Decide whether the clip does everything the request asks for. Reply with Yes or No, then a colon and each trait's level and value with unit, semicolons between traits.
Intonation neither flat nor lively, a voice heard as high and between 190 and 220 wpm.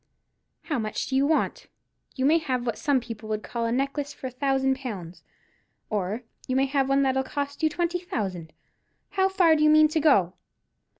Yes: average, 4.6 semitones; very high, 270 Hz; average, 195 wpm